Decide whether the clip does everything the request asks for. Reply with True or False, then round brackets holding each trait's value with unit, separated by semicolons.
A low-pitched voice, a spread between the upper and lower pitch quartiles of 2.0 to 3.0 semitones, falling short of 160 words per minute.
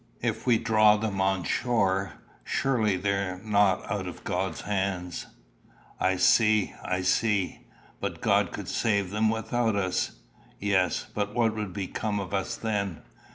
True (100 Hz; 2.5 semitones; 150 wpm)